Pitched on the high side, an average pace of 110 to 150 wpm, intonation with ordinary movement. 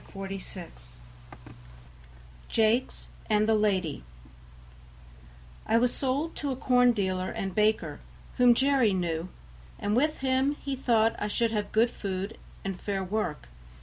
Yes: high, 215 Hz; average, 140 wpm; average, 4.4 semitones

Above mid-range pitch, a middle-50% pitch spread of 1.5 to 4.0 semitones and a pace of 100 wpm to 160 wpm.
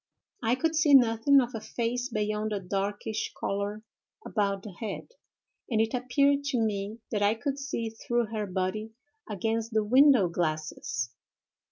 Yes: high, 220 Hz; average, 3.2 semitones; average, 155 wpm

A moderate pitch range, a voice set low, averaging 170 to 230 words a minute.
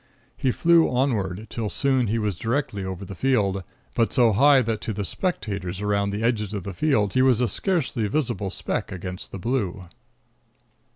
Yes: average, 4.7 semitones; low, 110 Hz; average, 180 wpm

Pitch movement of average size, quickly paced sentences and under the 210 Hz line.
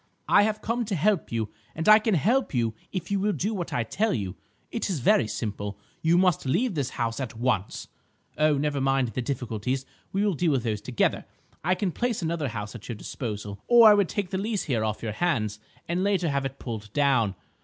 No: wide, 9.0 semitones; fast, 220 wpm; medium, 140 Hz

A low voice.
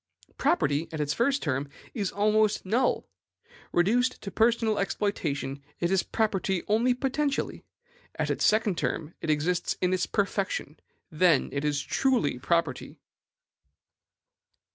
No: high, 190 Hz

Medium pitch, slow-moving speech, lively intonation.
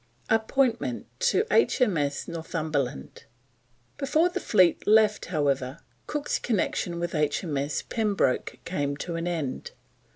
Yes: medium, 170 Hz; slow, 105 wpm; wide, 7.3 semitones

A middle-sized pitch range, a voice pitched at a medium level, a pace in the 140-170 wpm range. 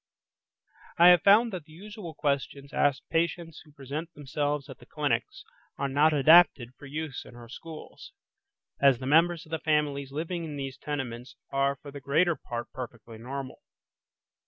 Yes: average, 3.1 semitones; medium, 145 Hz; average, 165 wpm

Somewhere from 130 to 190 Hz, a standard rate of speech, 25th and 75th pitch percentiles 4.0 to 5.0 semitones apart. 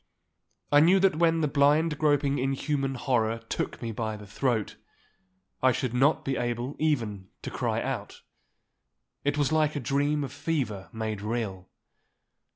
Yes: low, 135 Hz; average, 155 wpm; average, 4.5 semitones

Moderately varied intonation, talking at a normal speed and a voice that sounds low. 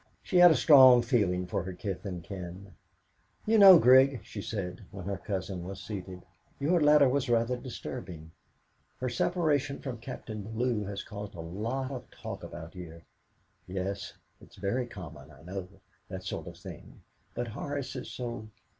No: wide, 5.8 semitones; average, 170 wpm; low, 105 Hz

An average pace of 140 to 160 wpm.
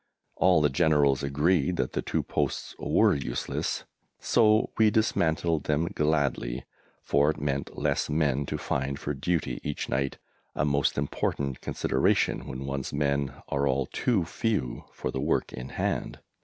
Yes: average, 155 wpm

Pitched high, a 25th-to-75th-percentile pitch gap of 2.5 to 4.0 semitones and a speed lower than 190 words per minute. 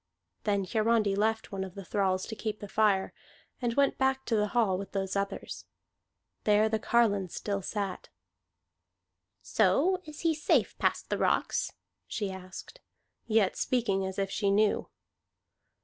Yes: high, 210 Hz; average, 2.9 semitones; average, 150 wpm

